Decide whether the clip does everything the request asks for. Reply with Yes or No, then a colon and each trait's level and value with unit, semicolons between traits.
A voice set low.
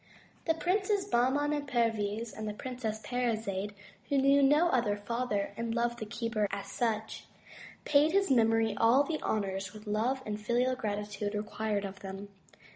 No: high, 225 Hz